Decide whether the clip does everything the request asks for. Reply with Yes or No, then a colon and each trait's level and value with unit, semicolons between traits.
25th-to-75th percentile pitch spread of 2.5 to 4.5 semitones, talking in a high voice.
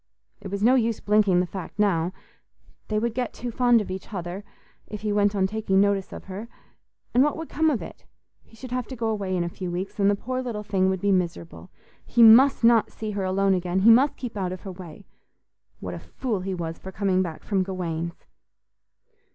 Yes: average, 3.4 semitones; high, 200 Hz